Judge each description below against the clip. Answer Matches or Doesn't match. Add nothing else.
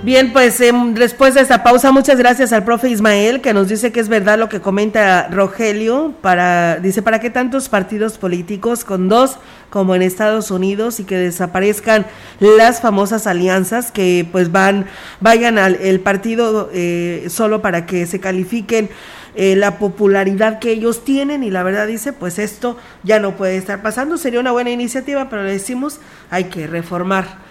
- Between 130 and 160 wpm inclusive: Doesn't match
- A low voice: Doesn't match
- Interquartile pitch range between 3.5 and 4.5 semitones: Matches